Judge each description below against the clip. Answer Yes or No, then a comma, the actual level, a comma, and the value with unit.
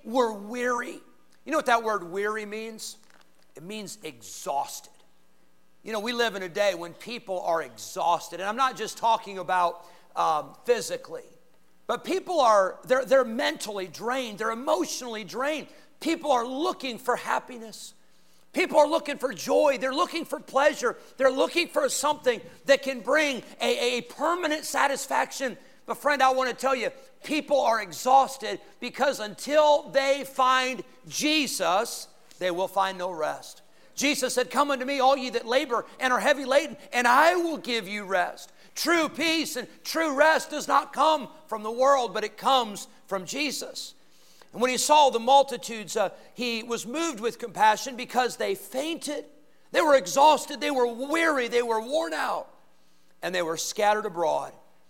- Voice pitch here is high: Yes, very high, 255 Hz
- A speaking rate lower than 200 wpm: Yes, average, 165 wpm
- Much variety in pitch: No, average, 4.9 semitones